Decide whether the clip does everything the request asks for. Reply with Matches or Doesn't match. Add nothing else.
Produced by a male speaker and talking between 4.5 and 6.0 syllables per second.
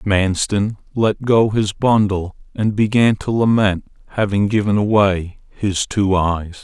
Doesn't match